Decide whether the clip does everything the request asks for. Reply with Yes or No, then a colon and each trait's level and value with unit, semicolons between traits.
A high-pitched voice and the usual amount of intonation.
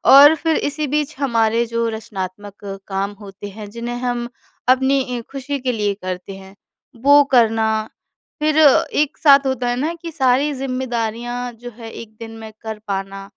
Yes: high, 240 Hz; average, 4.0 semitones